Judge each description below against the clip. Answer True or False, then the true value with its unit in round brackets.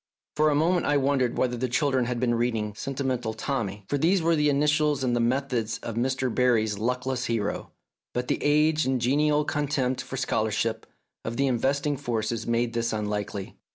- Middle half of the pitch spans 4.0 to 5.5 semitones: False (3.6 semitones)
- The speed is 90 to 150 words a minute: False (185 wpm)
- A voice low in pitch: True (125 Hz)